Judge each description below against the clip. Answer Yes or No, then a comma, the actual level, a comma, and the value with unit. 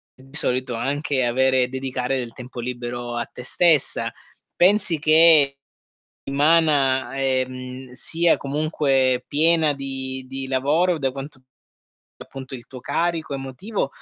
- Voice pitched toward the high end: No, low, 135 Hz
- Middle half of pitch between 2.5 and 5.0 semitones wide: Yes, average, 2.9 semitones